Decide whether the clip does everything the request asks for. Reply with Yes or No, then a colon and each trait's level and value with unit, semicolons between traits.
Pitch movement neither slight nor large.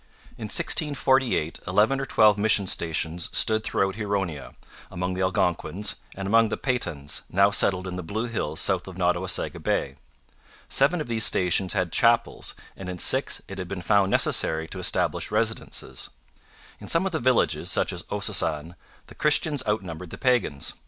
Yes: average, 4.4 semitones